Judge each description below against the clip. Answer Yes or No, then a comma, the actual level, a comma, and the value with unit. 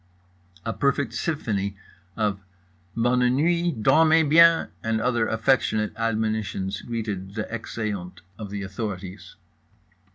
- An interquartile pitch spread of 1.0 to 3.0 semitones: No, average, 4.0 semitones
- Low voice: Yes, low, 115 Hz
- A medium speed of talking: No, slow, 105 wpm